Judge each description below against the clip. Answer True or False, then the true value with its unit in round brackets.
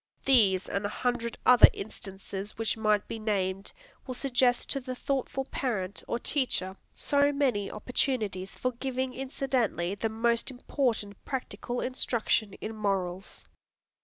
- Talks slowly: True (130 wpm)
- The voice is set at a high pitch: True (230 Hz)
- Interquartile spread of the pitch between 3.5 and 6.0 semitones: True (4.2 semitones)